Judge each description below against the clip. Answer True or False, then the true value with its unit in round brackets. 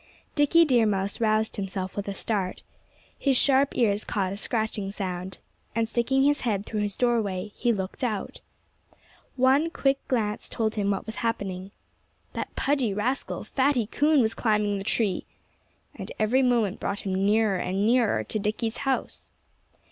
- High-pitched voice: True (220 Hz)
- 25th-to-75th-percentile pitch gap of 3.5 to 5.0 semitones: True (3.9 semitones)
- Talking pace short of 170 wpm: True (160 wpm)